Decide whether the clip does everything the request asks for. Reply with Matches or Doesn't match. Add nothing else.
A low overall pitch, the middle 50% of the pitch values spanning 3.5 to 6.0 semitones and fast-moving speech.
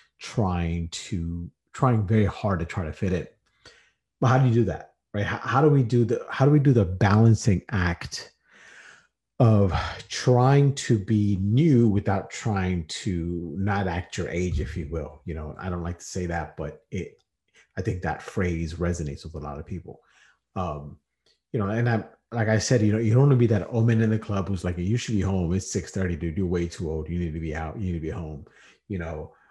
Matches